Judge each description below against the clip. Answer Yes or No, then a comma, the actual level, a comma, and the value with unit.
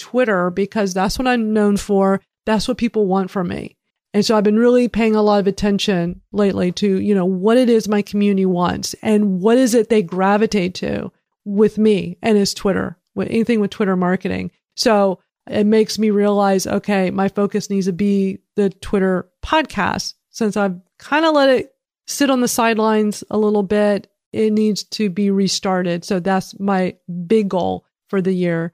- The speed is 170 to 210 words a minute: Yes, average, 190 wpm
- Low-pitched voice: No, high, 205 Hz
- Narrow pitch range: Yes, narrow, 2.2 semitones